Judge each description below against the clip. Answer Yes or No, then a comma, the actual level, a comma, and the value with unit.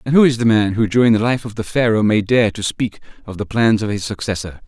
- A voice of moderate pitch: No, low, 110 Hz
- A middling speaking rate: No, fast, 280 wpm